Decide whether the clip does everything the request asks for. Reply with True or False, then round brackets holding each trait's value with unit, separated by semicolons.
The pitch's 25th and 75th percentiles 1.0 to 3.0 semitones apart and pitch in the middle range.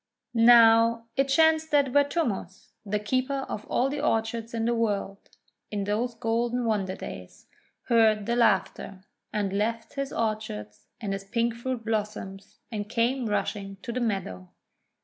False (2.7 semitones; 225 Hz)